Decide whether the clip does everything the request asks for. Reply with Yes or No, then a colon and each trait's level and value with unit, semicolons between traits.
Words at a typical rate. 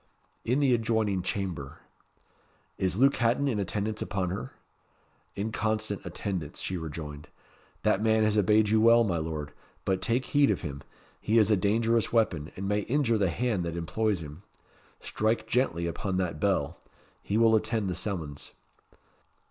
Yes: average, 160 wpm